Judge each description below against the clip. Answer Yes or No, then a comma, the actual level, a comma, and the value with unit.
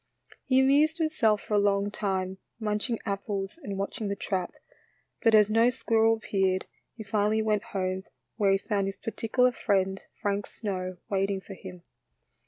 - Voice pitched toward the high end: Yes, high, 205 Hz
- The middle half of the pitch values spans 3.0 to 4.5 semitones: No, narrow, 2.4 semitones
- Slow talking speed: No, average, 165 wpm